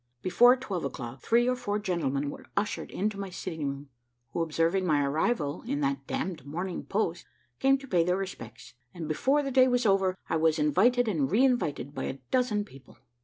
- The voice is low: No, medium, 185 Hz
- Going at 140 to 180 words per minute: No, average, 195 wpm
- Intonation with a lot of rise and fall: Yes, wide, 8.0 semitones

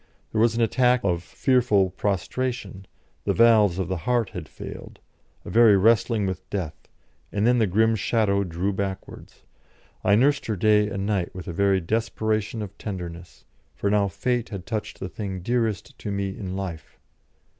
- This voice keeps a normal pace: Yes, average, 170 wpm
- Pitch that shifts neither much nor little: Yes, average, 3.2 semitones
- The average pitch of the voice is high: No, low, 100 Hz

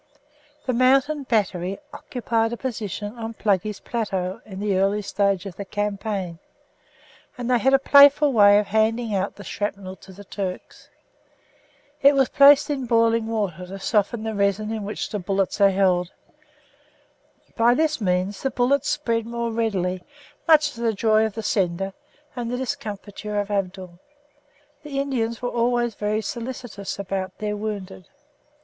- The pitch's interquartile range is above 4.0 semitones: No, average, 3.5 semitones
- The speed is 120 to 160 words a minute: Yes, average, 155 wpm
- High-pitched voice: Yes, high, 215 Hz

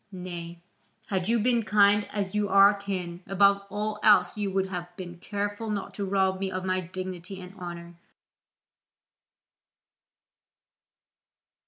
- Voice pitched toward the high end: Yes, high, 195 Hz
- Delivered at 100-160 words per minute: Yes, slow, 135 wpm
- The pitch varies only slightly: Yes, narrow, 2.1 semitones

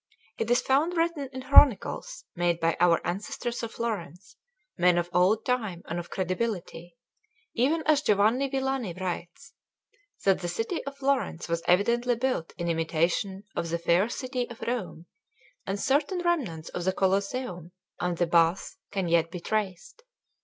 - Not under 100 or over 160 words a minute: Yes, average, 155 wpm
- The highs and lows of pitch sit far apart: Yes, wide, 6.6 semitones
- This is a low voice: No, high, 200 Hz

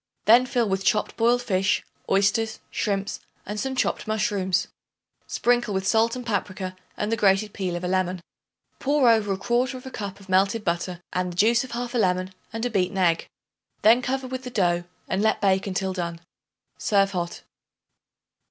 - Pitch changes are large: No, average, 3.9 semitones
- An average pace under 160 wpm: No, average, 170 wpm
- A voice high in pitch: Yes, high, 200 Hz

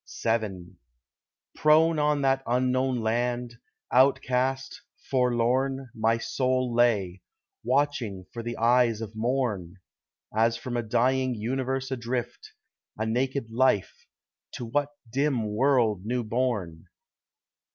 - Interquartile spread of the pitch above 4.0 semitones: No, average, 2.7 semitones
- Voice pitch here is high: No, low, 120 Hz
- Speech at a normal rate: No, slow, 105 wpm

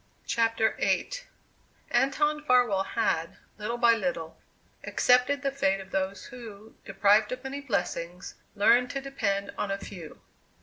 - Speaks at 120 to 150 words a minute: Yes, slow, 135 wpm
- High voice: Yes, high, 220 Hz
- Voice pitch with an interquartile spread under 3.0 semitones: No, average, 4.4 semitones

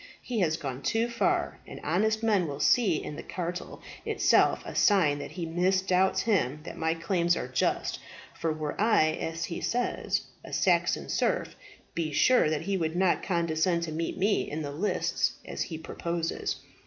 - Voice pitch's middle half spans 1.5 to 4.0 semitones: Yes, average, 3.6 semitones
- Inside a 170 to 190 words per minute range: Yes, average, 180 wpm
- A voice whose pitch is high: No, medium, 170 Hz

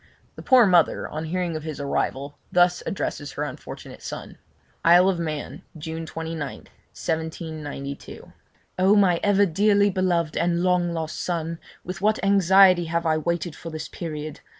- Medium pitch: Yes, medium, 170 Hz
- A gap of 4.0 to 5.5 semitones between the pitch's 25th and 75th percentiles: No, narrow, 2.6 semitones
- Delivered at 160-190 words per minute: No, average, 150 wpm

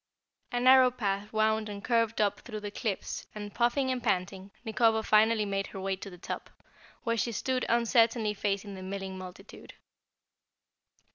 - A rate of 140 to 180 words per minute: Yes, average, 160 wpm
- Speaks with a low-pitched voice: No, high, 215 Hz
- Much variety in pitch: No, average, 2.8 semitones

